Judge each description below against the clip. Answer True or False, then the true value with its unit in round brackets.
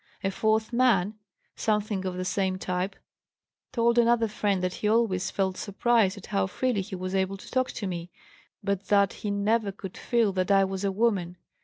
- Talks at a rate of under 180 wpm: False (190 wpm)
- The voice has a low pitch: False (200 Hz)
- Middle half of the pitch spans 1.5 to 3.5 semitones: True (2.7 semitones)